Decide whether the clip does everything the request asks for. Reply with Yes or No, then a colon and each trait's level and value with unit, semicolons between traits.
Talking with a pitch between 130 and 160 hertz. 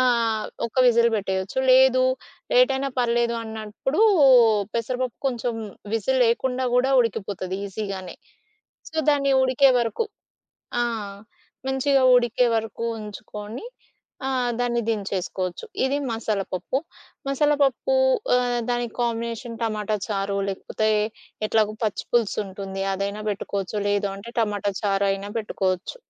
No: high, 225 Hz